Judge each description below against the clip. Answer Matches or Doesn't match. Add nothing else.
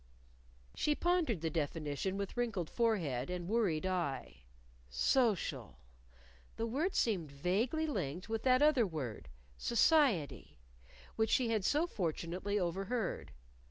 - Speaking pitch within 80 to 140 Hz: Doesn't match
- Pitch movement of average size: Doesn't match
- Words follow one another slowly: Matches